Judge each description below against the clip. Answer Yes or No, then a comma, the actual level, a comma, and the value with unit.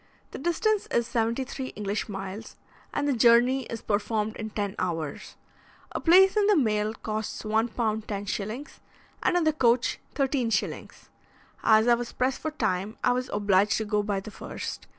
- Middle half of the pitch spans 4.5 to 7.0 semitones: No, average, 3.8 semitones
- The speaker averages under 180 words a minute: Yes, average, 170 wpm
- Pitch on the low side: No, high, 225 Hz